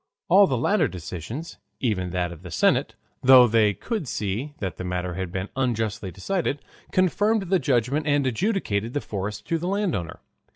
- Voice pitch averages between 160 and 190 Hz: No, low, 120 Hz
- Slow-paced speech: No, average, 170 wpm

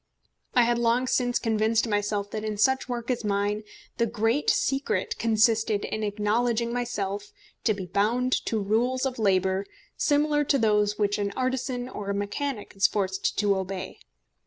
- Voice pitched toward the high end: Yes, high, 220 Hz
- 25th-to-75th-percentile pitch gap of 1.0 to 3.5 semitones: Yes, average, 3.1 semitones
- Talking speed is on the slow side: No, average, 160 wpm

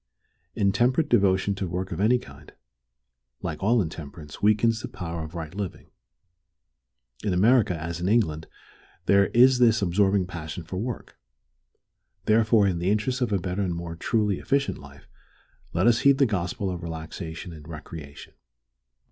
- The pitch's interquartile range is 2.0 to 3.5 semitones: No, average, 4.6 semitones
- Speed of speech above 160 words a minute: No, average, 155 wpm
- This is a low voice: Yes, very low, 95 Hz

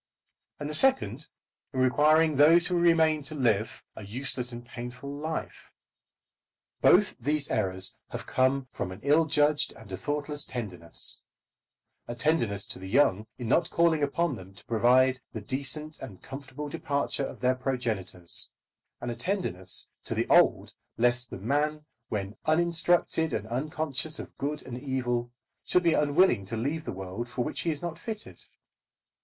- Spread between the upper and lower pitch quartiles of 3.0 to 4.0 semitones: No, average, 4.7 semitones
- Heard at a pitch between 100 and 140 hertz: Yes, low, 135 Hz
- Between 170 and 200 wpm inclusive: No, average, 160 wpm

